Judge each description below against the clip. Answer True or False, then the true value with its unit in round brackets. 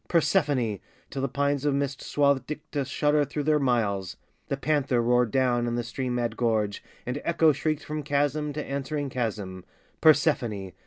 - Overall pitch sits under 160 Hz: True (135 Hz)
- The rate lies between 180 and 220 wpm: False (165 wpm)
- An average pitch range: True (3.6 semitones)